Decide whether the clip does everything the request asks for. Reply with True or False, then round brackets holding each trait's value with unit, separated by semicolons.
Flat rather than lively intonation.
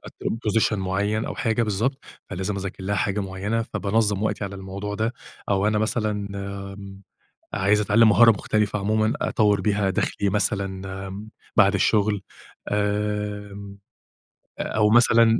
True (1.5 semitones)